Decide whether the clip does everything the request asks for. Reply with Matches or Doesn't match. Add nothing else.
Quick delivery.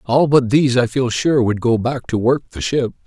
Matches